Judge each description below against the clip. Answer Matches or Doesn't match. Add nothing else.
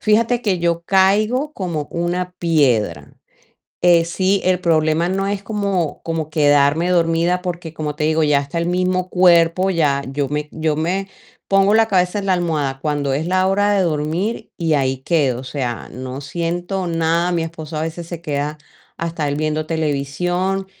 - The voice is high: Doesn't match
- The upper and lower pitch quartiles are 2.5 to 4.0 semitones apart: Matches